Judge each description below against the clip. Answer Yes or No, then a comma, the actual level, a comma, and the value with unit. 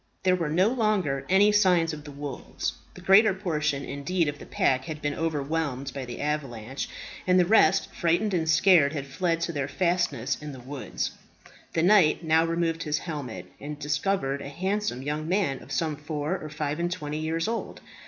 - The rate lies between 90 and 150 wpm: No, average, 190 wpm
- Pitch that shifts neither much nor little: Yes, average, 4.0 semitones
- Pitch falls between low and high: Yes, medium, 155 Hz